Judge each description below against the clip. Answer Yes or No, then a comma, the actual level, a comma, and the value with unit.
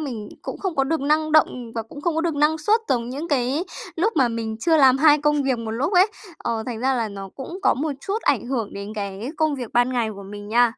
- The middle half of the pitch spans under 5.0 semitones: No, average, 5.3 semitones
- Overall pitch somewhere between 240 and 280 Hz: Yes, very high, 265 Hz